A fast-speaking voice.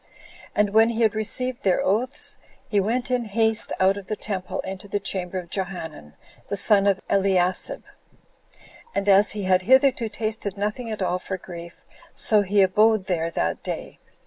No: average, 175 wpm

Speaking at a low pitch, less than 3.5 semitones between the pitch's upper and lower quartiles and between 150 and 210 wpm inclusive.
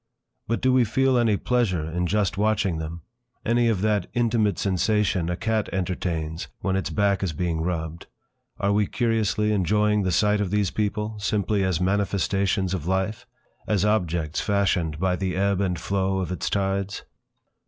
Yes: low, 100 Hz; average, 2.9 semitones; average, 165 wpm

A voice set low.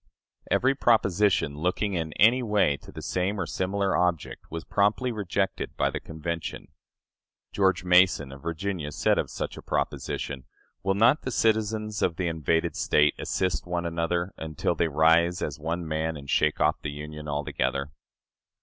Yes: very low, 85 Hz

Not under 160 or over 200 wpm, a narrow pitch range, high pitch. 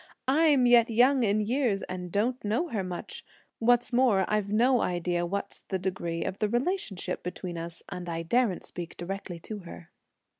No: average, 175 wpm; average, 5.3 semitones; high, 205 Hz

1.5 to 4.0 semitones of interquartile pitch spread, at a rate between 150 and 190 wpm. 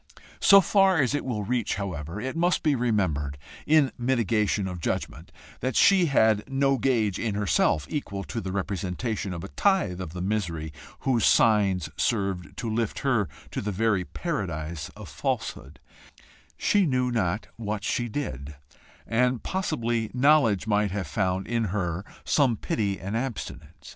No: average, 5.3 semitones; average, 155 wpm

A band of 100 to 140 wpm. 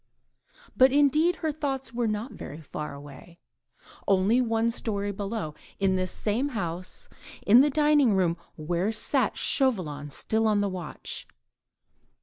Yes: slow, 135 wpm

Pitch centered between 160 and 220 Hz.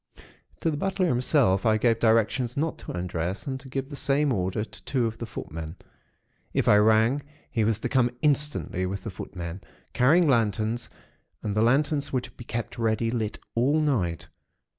No: low, 115 Hz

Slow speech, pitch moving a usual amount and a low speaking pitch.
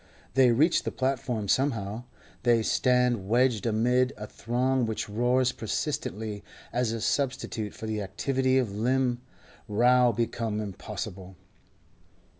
Yes: slow, 120 wpm; average, 3.0 semitones; low, 120 Hz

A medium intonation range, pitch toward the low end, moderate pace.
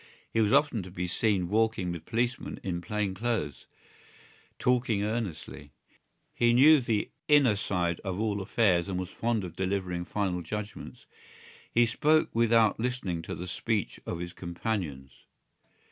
Yes: average, 4.5 semitones; low, 100 Hz; average, 145 wpm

